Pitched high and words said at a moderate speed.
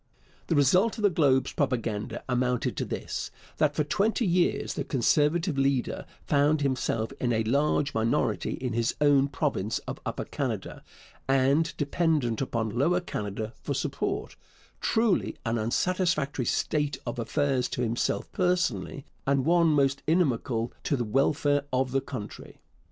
No: medium, 140 Hz; average, 145 wpm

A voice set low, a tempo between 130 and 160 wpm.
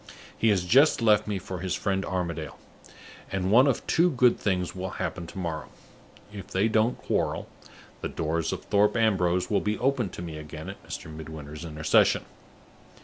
No: very low, 95 Hz; average, 175 wpm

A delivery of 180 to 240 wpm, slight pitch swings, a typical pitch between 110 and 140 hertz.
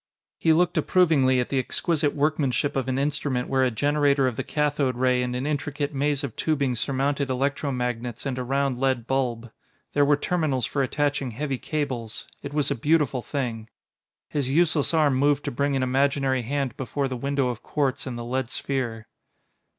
Yes: average, 185 wpm; narrow, 2.3 semitones; low, 135 Hz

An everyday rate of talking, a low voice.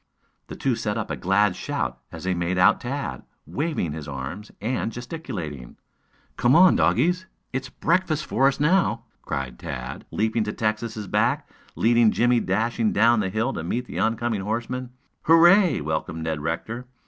Yes: average, 160 wpm; low, 115 Hz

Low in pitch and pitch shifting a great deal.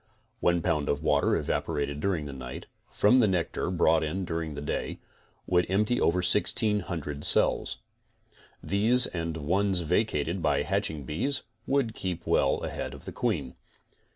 No: very low, 85 Hz; average, 4.7 semitones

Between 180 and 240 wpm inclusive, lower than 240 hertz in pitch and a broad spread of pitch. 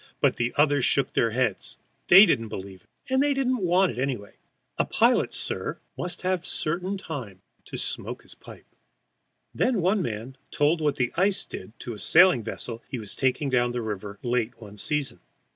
Yes: average, 185 wpm; low, 135 Hz; wide, 7.7 semitones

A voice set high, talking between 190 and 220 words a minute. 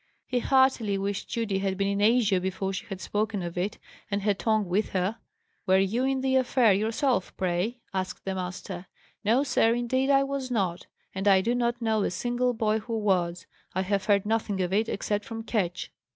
Yes: high, 210 Hz; average, 200 wpm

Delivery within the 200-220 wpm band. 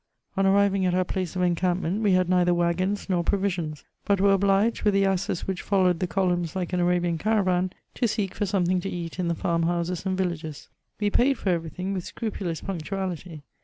Yes: fast, 205 wpm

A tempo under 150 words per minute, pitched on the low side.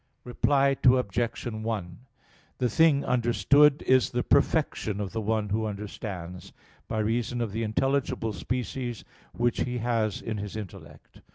Yes: average, 140 wpm; low, 115 Hz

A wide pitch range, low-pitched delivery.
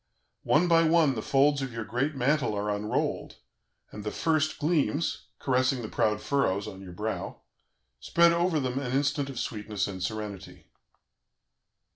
Yes: wide, 5.7 semitones; low, 130 Hz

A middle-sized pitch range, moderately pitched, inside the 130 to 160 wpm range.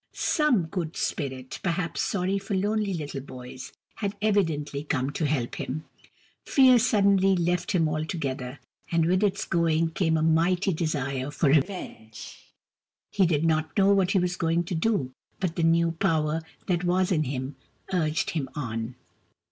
Yes: average, 4.1 semitones; medium, 165 Hz; average, 155 wpm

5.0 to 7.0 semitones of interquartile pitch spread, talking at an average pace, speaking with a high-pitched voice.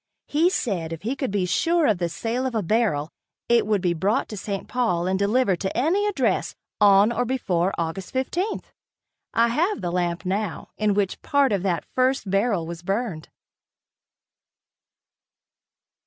Yes: wide, 5.6 semitones; average, 165 wpm; high, 205 Hz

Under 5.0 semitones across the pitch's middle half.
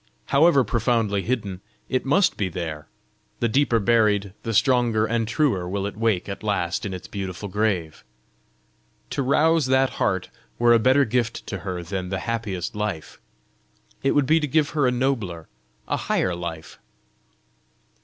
No: average, 5.3 semitones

